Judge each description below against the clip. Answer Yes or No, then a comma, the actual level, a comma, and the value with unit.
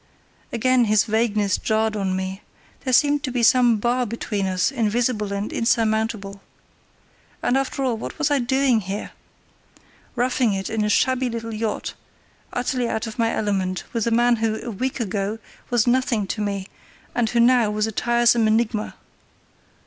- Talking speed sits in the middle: Yes, average, 165 wpm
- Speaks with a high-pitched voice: Yes, high, 225 Hz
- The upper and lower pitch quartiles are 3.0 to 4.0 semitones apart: No, narrow, 2.6 semitones